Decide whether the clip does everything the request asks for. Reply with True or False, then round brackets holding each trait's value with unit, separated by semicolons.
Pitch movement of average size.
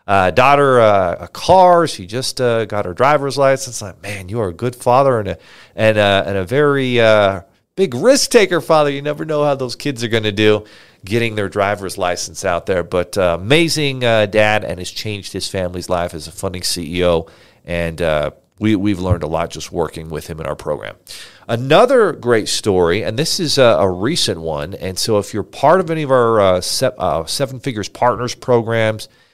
False (5.9 semitones)